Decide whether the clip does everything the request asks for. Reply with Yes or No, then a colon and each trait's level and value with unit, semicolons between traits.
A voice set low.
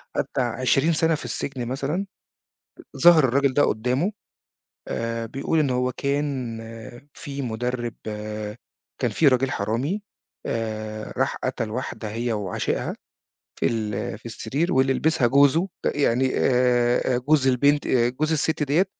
Yes: low, 130 Hz